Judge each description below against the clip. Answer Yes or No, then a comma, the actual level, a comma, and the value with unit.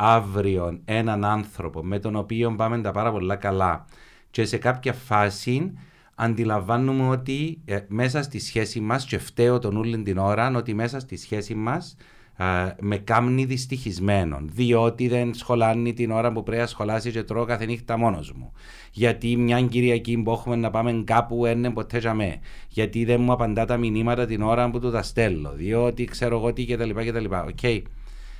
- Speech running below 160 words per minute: No, fast, 170 wpm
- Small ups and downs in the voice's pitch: Yes, narrow, 2.2 semitones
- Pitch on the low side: Yes, low, 115 Hz